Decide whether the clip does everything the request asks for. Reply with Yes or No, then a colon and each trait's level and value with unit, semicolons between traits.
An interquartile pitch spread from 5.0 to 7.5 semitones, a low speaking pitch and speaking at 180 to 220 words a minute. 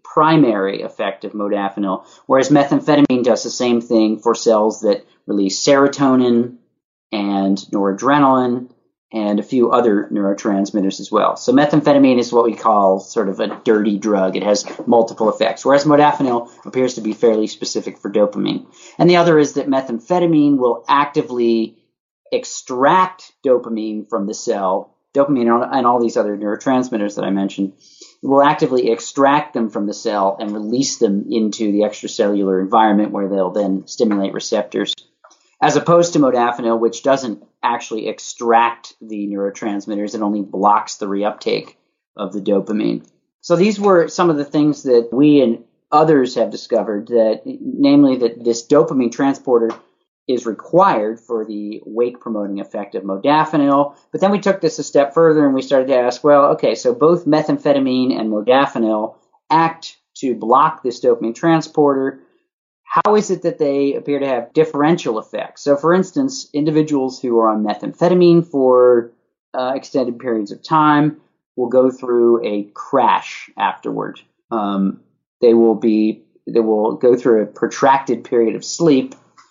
No: average, 5.3 semitones; low, 120 Hz; average, 155 wpm